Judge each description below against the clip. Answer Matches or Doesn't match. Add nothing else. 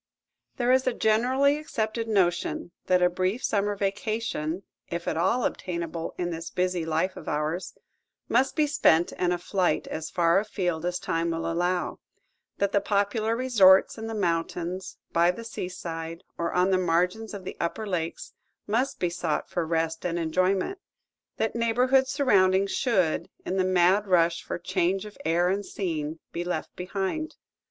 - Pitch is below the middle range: Doesn't match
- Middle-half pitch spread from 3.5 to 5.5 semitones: Matches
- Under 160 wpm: Doesn't match